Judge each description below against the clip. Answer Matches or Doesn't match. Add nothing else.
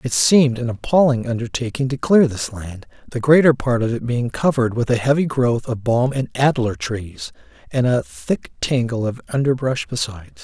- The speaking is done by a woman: Doesn't match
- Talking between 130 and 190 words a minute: Matches